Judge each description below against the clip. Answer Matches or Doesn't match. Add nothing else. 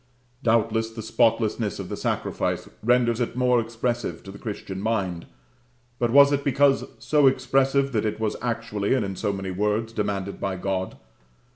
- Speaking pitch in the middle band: Doesn't match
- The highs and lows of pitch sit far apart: Doesn't match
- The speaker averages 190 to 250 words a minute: Doesn't match